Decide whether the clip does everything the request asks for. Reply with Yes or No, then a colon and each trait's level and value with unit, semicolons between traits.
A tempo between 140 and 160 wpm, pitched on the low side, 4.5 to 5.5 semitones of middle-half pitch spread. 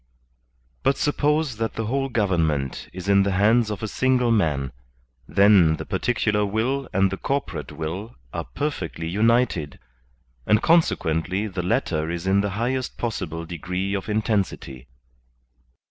Yes: average, 145 wpm; low, 100 Hz; average, 5.2 semitones